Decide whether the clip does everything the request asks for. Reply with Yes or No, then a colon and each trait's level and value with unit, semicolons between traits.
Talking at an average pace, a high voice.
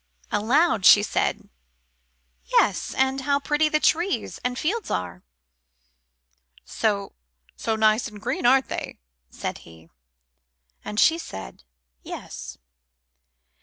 No: slow, 115 wpm; high, 220 Hz